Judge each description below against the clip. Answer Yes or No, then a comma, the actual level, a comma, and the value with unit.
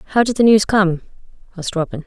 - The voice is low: No, high, 195 Hz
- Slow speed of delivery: No, fast, 205 wpm